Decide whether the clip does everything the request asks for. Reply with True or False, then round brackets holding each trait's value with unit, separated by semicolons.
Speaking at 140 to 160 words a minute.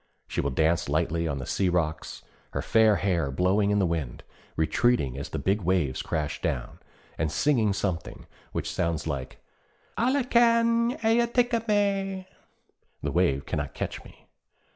True (155 wpm)